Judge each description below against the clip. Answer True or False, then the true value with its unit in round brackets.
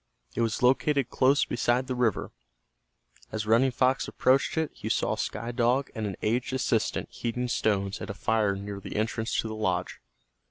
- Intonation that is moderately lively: True (3.1 semitones)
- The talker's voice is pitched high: False (115 Hz)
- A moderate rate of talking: True (175 wpm)